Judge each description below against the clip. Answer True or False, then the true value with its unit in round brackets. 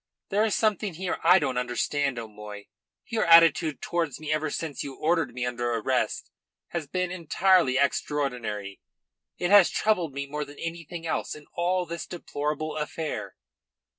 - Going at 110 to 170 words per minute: True (155 wpm)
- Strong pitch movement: False (4.5 semitones)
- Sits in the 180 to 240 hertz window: False (155 Hz)